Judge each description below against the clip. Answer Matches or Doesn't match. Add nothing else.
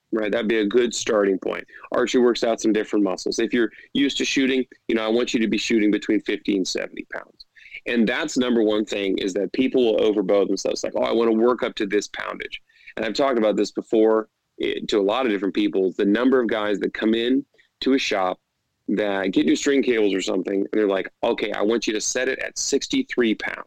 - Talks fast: Matches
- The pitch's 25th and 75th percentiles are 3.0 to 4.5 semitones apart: Matches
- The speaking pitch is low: Matches